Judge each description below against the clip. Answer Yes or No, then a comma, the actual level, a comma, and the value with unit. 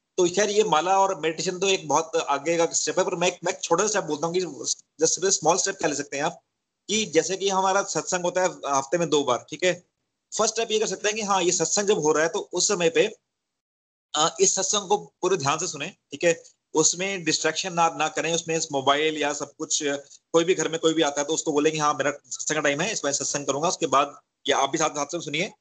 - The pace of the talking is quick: Yes, fast, 250 wpm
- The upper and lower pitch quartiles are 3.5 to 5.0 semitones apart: Yes, average, 4.0 semitones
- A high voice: No, medium, 165 Hz